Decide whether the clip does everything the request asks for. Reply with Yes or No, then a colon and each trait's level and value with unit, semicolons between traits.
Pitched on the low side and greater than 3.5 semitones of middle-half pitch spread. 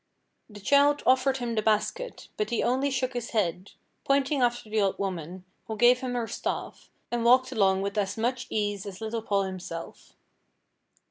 No: high, 225 Hz; average, 4.3 semitones